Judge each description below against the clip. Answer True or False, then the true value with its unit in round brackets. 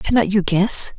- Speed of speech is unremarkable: True (185 wpm)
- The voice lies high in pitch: True (200 Hz)